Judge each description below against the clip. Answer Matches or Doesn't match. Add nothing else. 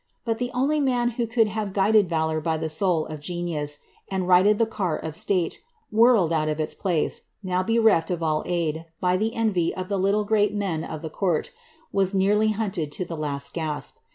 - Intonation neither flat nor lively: Matches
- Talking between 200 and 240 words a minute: Matches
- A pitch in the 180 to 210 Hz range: Matches